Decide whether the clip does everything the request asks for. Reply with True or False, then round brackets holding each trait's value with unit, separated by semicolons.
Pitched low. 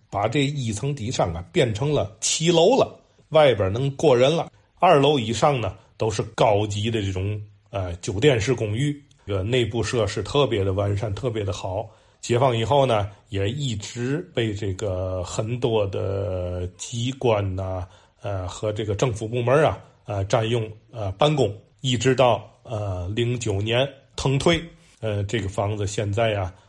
True (110 Hz)